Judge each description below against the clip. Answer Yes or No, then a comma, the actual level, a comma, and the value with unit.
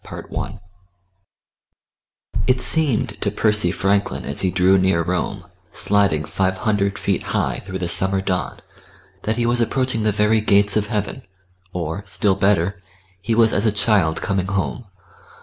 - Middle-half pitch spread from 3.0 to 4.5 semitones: No, narrow, 2.5 semitones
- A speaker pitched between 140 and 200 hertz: No, low, 100 Hz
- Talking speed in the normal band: Yes, average, 160 wpm